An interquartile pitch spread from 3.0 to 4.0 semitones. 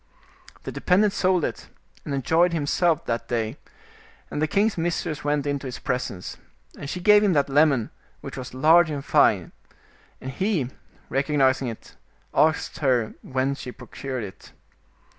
No: average, 4.4 semitones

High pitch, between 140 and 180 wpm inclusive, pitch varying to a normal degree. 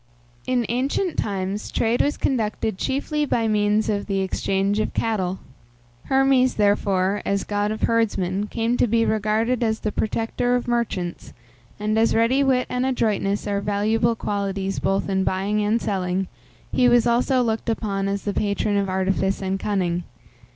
Yes: high, 210 Hz; average, 160 wpm; average, 3.0 semitones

